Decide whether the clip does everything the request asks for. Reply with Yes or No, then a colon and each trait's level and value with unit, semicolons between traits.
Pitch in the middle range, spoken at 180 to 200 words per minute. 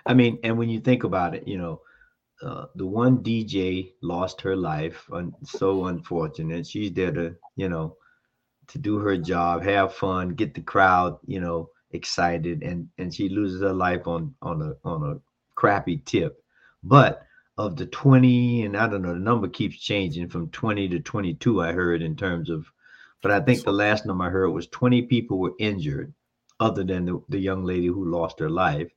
No: very low, 95 Hz; average, 195 wpm